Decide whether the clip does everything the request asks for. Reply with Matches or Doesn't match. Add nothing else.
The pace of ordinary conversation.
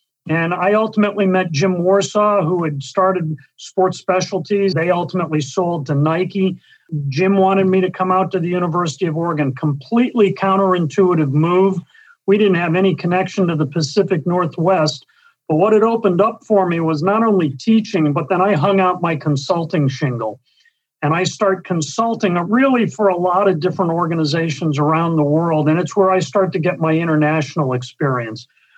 Matches